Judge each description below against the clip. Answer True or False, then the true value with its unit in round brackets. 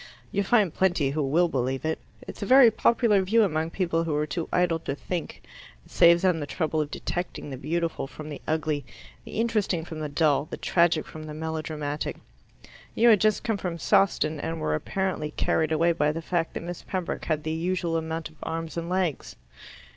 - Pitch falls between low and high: True (165 Hz)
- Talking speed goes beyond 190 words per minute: True (200 wpm)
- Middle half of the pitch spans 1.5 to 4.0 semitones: True (2.9 semitones)